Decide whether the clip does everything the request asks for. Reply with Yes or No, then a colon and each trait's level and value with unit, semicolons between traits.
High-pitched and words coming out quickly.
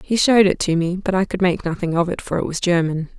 No: medium, 180 Hz; fast, 300 wpm